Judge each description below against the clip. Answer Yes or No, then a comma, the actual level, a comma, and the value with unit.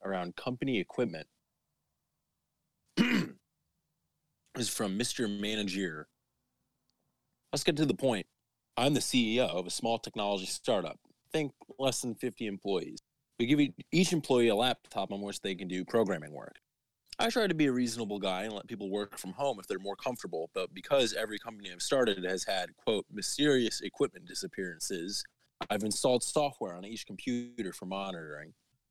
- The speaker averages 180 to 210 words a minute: No, average, 160 wpm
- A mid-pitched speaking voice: No, low, 110 Hz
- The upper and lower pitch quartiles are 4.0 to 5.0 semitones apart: Yes, average, 4.5 semitones